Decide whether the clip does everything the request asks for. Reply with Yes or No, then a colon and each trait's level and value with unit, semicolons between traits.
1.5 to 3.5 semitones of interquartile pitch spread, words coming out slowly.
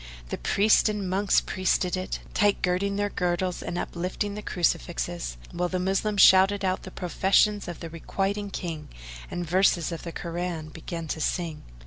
No: narrow, 2.5 semitones; average, 165 wpm